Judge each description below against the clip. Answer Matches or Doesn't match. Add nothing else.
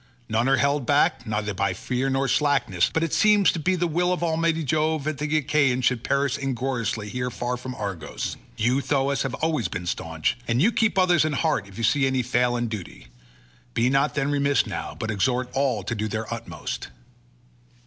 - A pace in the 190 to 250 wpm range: Matches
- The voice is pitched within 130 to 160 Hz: Matches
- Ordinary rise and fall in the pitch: Matches